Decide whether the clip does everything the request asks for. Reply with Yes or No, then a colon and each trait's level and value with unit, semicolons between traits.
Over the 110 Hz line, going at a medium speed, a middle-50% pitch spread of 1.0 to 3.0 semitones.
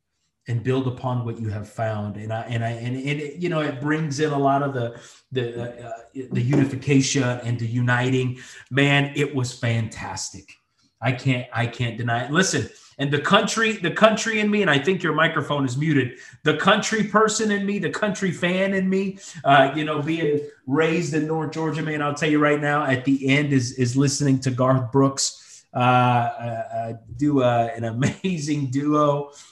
No: medium, 140 Hz; average, 190 wpm; average, 3.9 semitones